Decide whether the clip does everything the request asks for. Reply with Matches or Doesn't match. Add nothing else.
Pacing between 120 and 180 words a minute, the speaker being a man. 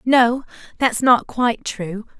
Doesn't match